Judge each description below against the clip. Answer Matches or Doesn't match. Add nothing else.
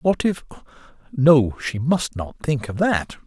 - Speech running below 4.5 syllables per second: Matches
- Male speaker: Matches